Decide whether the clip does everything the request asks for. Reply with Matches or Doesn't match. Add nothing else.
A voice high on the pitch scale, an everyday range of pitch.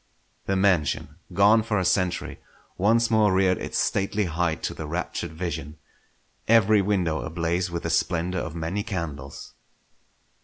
Doesn't match